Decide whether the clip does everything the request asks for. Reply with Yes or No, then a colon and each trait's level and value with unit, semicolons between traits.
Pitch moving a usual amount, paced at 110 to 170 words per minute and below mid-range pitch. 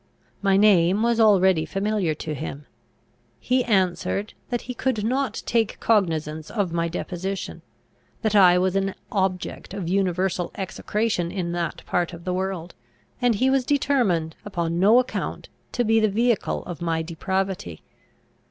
No: average, 4.0 semitones; average, 150 wpm; high, 190 Hz